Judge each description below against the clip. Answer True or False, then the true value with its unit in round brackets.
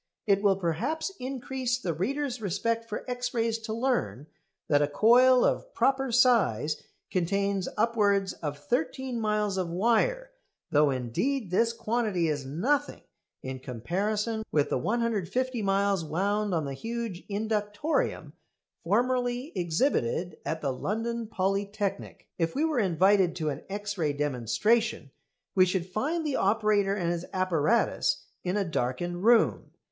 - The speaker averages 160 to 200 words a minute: False (140 wpm)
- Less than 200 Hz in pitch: False (205 Hz)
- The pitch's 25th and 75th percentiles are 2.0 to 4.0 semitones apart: False (5.6 semitones)